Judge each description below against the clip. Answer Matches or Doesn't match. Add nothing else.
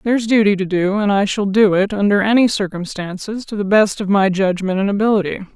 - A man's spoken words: Doesn't match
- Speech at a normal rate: Doesn't match